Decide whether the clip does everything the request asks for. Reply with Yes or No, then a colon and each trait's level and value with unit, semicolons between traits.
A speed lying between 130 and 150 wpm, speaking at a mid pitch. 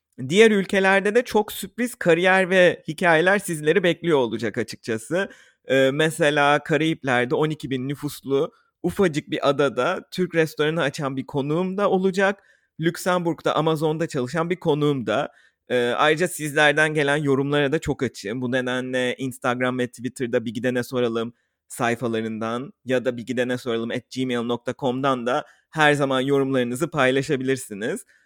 Yes: average, 135 wpm; medium, 145 Hz